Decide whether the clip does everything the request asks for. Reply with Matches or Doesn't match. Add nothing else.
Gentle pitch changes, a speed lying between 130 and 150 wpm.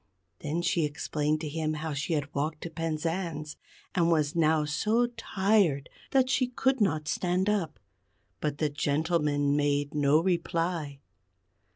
Doesn't match